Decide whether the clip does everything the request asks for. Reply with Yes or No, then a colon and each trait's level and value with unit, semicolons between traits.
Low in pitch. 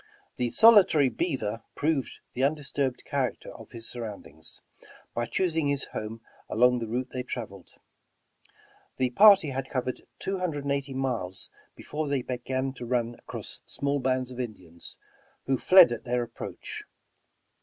Yes: low, 130 Hz